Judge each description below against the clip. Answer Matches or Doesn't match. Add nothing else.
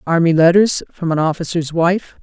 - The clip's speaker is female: Matches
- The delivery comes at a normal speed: Matches